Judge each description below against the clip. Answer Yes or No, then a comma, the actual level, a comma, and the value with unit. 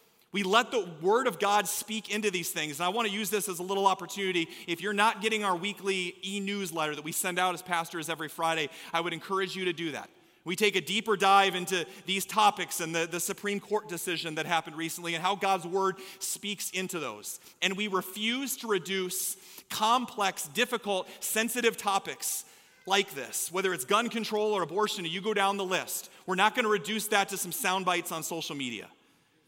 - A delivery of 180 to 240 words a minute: Yes, fast, 205 wpm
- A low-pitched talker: No, high, 190 Hz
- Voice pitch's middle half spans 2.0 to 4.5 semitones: Yes, average, 2.9 semitones